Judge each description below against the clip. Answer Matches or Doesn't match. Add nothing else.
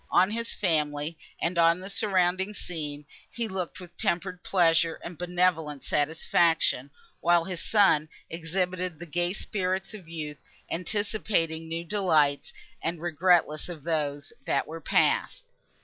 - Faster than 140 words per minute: Doesn't match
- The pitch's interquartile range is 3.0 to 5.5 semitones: Doesn't match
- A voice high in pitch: Doesn't match